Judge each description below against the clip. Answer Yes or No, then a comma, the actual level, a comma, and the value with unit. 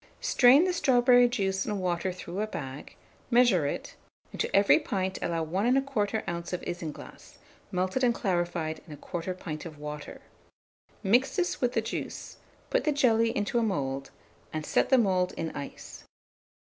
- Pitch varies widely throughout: Yes, wide, 6.1 semitones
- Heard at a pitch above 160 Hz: Yes, high, 190 Hz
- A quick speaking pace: No, average, 165 wpm